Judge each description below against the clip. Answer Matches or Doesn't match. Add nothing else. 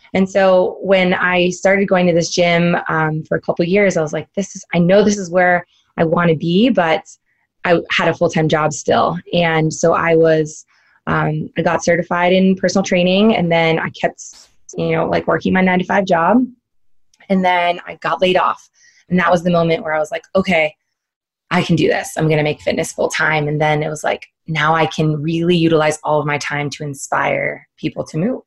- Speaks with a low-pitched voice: Doesn't match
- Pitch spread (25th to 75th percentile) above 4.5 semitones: Doesn't match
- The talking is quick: Matches